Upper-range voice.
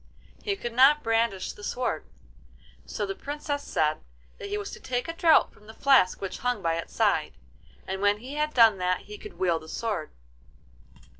Yes: high, 225 Hz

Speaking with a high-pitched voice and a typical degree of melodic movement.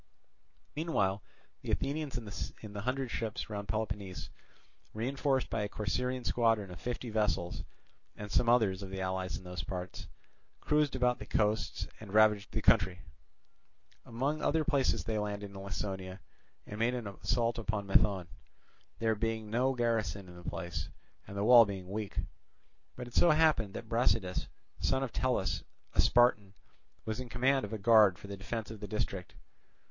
No: low, 110 Hz; average, 3.8 semitones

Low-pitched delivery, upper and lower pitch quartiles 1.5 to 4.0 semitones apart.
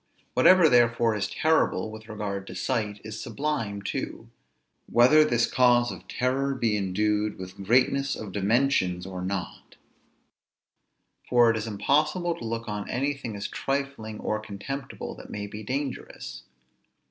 No: low, 115 Hz; average, 4.7 semitones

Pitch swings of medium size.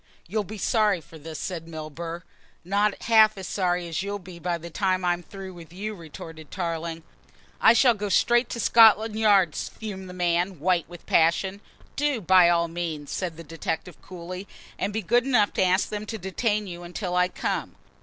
Yes: average, 3.5 semitones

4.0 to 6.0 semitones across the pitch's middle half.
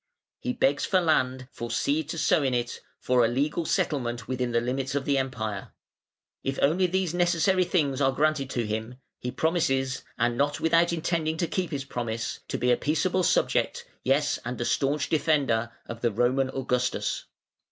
Yes: average, 4.4 semitones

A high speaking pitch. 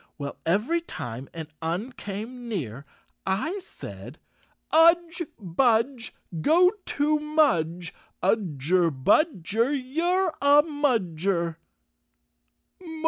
Yes: high, 230 Hz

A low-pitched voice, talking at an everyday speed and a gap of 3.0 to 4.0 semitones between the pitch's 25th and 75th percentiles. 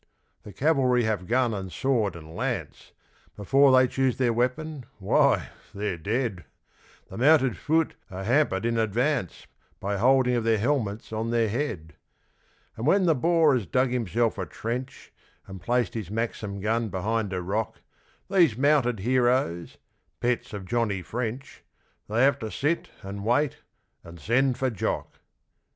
No: low, 120 Hz; average, 150 wpm; average, 4.4 semitones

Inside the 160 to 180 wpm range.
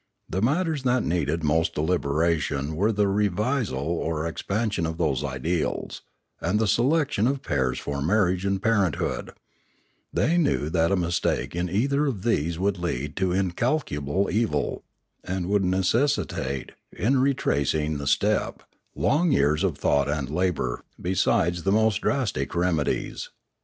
No: average, 140 wpm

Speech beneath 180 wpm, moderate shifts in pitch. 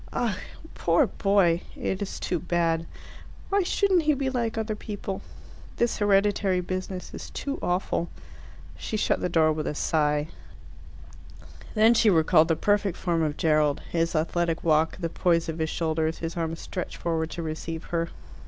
Yes: average, 160 wpm; average, 3.9 semitones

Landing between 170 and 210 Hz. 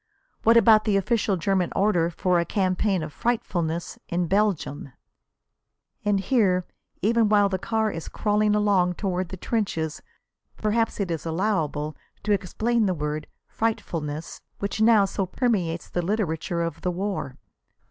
Yes: high, 190 Hz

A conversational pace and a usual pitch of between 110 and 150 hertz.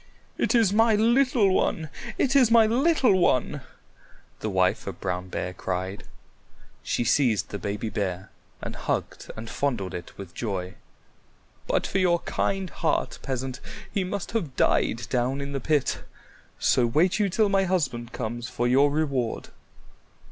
Yes: average, 155 wpm; medium, 140 Hz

